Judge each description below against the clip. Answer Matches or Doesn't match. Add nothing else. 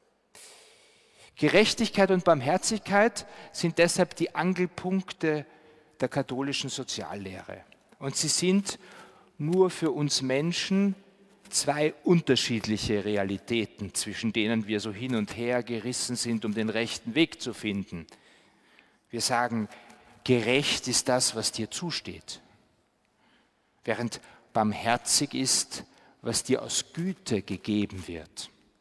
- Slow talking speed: Matches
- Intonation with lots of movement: Matches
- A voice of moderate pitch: Doesn't match